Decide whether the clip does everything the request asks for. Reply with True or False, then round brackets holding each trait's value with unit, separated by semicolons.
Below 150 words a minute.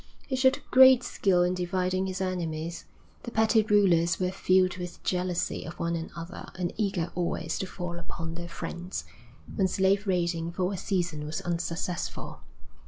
False (160 wpm)